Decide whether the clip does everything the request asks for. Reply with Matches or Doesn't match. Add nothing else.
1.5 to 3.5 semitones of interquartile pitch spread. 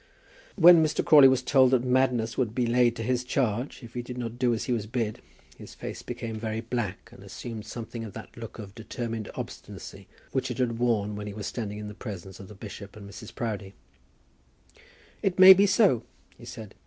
Matches